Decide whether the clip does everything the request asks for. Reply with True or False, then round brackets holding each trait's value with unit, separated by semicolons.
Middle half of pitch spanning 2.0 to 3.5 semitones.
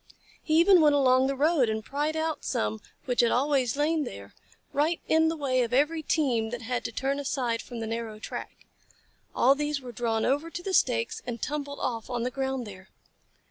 False (4.2 semitones)